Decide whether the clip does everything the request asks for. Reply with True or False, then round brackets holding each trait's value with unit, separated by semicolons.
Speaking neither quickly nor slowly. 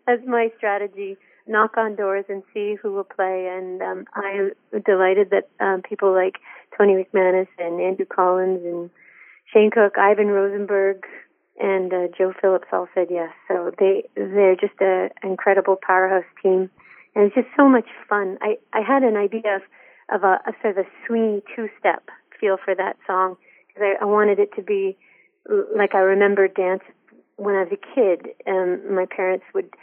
True (175 wpm)